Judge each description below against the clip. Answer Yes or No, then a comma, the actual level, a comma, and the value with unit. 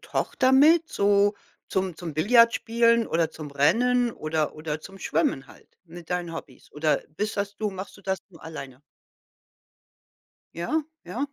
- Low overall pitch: No, high, 190 Hz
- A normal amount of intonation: No, wide, 6.4 semitones